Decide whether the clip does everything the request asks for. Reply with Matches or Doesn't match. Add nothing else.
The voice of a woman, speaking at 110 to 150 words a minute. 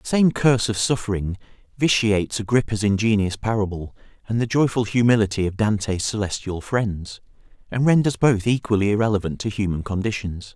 Doesn't match